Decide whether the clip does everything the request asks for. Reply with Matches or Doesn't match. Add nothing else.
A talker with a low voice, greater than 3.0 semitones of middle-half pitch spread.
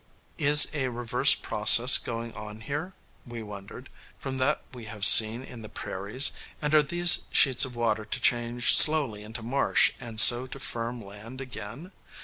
Matches